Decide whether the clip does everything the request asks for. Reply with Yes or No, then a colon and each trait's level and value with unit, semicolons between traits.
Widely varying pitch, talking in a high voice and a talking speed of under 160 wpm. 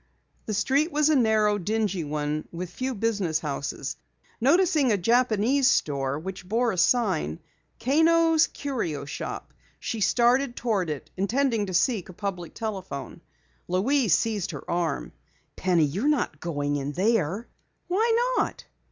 Yes: wide, 7.1 semitones; high, 210 Hz; average, 140 wpm